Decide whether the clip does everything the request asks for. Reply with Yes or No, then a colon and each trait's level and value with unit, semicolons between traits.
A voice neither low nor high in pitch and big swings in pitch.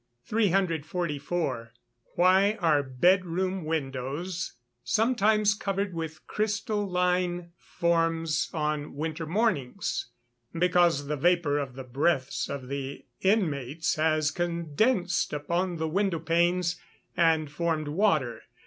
No: medium, 170 Hz; average, 3.7 semitones